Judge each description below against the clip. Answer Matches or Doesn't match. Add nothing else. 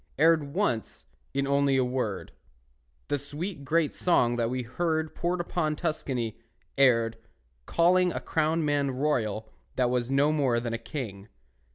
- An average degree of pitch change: Matches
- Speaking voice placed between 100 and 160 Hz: Matches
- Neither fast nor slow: Matches